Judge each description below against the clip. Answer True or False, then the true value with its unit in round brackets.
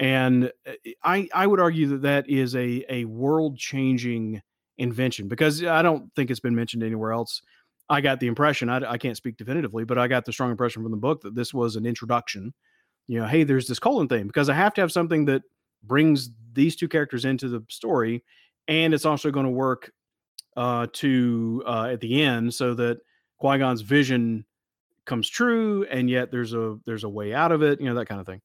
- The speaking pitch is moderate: False (125 Hz)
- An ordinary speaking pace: False (215 wpm)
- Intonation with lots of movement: False (3.7 semitones)